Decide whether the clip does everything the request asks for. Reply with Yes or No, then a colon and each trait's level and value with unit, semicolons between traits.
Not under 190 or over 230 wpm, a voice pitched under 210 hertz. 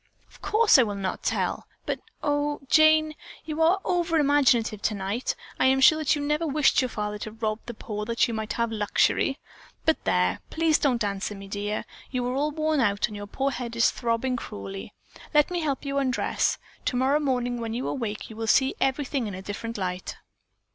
No: average, 200 wpm; high, 245 Hz